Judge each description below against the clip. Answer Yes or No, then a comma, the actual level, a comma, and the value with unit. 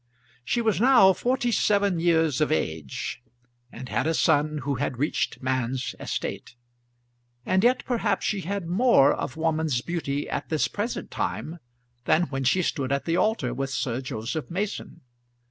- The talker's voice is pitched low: No, medium, 160 Hz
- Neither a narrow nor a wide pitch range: No, wide, 6.6 semitones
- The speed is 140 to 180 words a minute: Yes, average, 160 wpm